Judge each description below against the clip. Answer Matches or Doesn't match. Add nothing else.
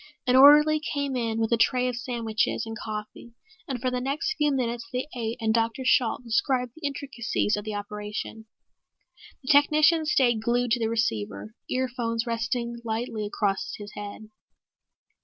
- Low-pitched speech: Doesn't match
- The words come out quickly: Doesn't match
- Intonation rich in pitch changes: Doesn't match